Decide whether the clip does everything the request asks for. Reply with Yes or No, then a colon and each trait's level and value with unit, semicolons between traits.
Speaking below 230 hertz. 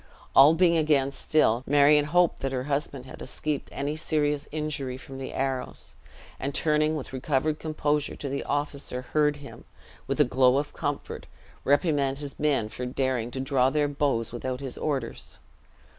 Yes: medium, 140 Hz